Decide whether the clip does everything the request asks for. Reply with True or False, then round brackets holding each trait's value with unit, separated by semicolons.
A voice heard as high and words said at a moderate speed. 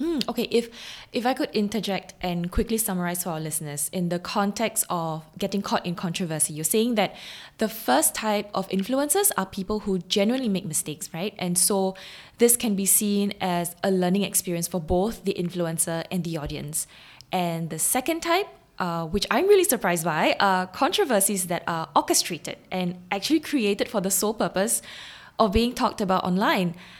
True (195 Hz; 175 wpm)